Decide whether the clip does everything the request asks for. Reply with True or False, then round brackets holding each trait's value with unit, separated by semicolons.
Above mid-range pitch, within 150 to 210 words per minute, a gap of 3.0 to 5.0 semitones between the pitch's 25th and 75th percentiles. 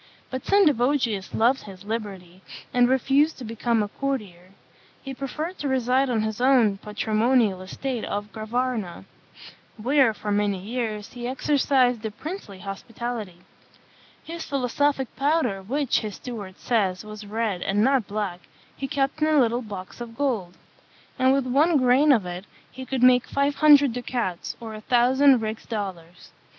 True (240 Hz; 155 wpm; 4.4 semitones)